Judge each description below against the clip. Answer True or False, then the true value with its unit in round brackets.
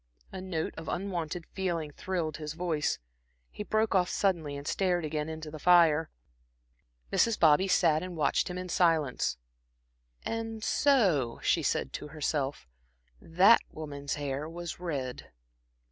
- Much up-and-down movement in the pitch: False (3.5 semitones)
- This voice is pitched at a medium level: True (165 Hz)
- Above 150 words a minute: False (140 wpm)